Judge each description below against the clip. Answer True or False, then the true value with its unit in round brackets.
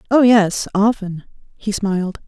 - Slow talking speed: True (130 wpm)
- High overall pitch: True (205 Hz)